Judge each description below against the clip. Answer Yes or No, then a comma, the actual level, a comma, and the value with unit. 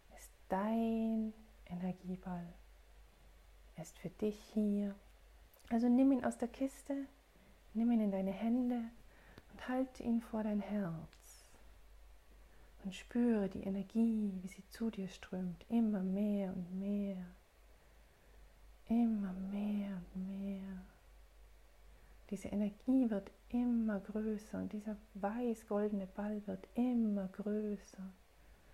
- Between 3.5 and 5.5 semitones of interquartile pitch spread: No, average, 2.9 semitones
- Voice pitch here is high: Yes, high, 205 Hz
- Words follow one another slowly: Yes, slow, 110 wpm